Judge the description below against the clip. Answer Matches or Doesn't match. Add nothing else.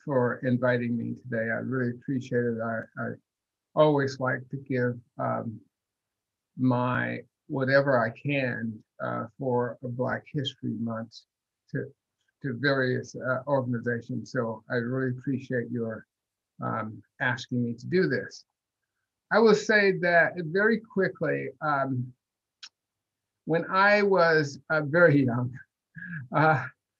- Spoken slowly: Matches